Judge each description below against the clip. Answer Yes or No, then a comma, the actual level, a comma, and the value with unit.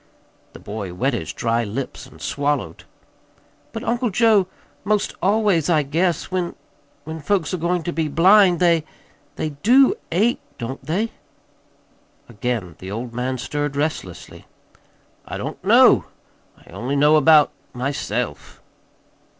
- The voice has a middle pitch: Yes, medium, 150 Hz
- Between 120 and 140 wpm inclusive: Yes, slow, 135 wpm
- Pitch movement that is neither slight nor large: No, wide, 6.7 semitones